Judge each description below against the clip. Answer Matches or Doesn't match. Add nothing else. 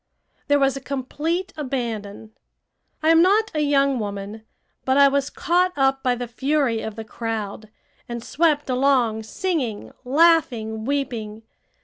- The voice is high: Matches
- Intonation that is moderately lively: Matches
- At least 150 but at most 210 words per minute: Doesn't match